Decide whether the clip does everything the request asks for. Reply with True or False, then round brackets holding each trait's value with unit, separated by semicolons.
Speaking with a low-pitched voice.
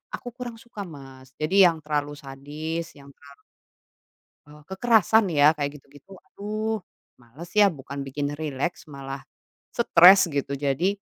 False (150 Hz)